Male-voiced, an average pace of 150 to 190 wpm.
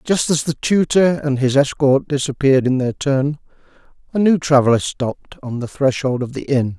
Yes: male; average, 185 wpm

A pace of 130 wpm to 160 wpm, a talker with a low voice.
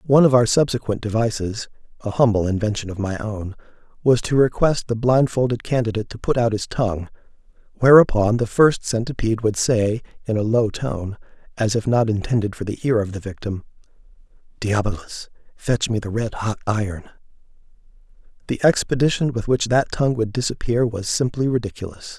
Yes: average, 155 wpm; low, 115 Hz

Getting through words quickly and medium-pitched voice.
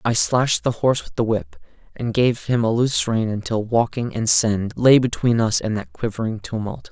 No: fast, 210 wpm; low, 115 Hz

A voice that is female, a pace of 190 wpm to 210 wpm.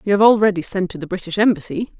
No: female; fast, 240 wpm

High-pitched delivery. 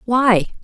Yes: high, 225 Hz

